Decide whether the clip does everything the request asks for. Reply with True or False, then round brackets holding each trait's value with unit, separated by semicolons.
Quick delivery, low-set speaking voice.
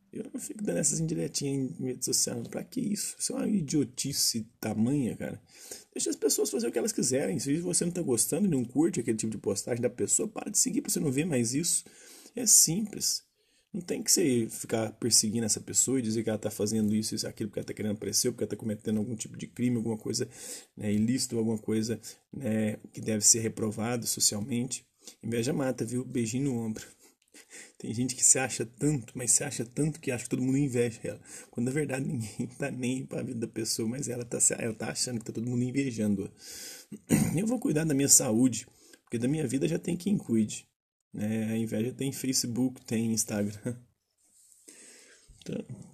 True (210 wpm; 125 Hz)